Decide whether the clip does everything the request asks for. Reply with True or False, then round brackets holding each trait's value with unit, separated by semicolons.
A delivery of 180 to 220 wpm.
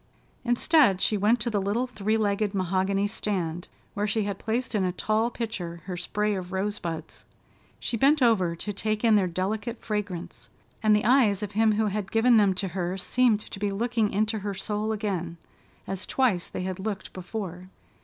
True (185 wpm)